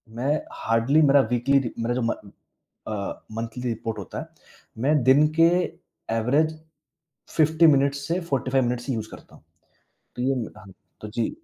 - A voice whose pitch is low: Yes, low, 130 Hz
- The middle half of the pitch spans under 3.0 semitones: No, average, 3.8 semitones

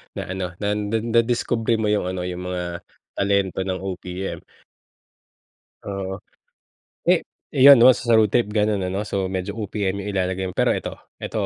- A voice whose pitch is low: Yes, low, 100 Hz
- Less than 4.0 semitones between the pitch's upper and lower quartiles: Yes, average, 2.8 semitones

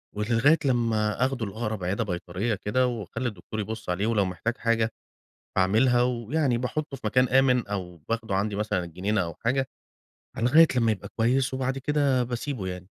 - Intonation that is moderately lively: Yes, average, 3.7 semitones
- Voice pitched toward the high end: No, low, 115 Hz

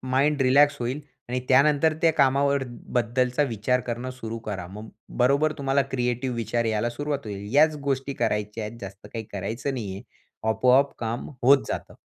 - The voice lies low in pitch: Yes, low, 125 Hz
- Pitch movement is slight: No, average, 3.6 semitones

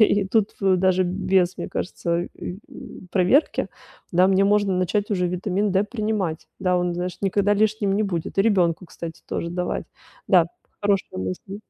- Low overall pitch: No, high, 190 Hz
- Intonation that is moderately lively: No, narrow, 2.3 semitones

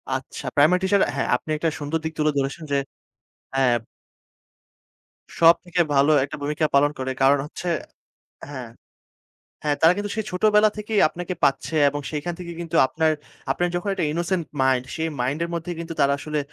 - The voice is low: No, medium, 160 Hz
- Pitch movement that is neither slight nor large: Yes, average, 3.8 semitones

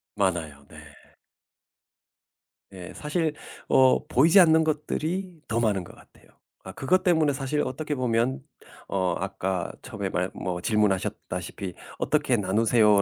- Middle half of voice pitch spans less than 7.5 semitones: No, wide, 7.9 semitones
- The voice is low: Yes, low, 115 Hz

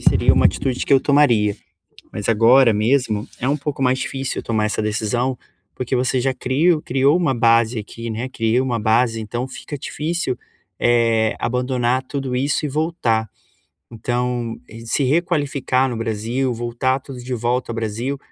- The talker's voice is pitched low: Yes, low, 125 Hz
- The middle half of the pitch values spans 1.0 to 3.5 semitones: Yes, average, 2.8 semitones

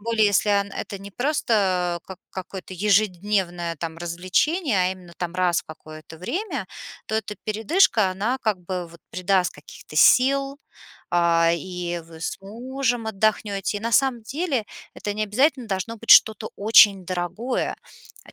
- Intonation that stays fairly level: No, average, 4.3 semitones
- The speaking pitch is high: Yes, high, 200 Hz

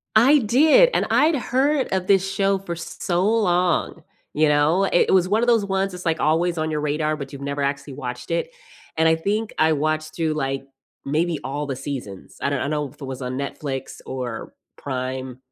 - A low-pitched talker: No, medium, 155 Hz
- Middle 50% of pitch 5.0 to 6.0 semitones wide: Yes, wide, 5.5 semitones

